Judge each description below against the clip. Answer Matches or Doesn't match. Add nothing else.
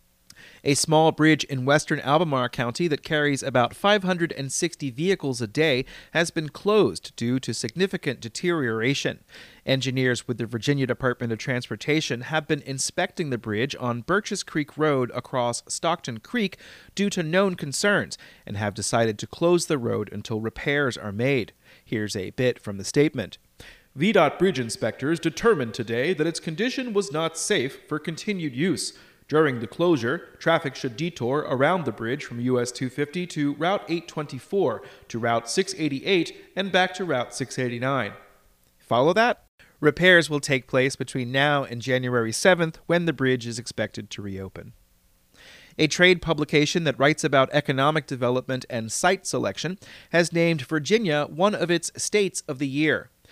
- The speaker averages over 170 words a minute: Doesn't match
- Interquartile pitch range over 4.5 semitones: Matches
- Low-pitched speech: Doesn't match